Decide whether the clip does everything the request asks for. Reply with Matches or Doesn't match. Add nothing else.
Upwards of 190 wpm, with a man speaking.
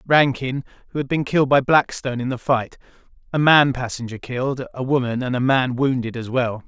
Matches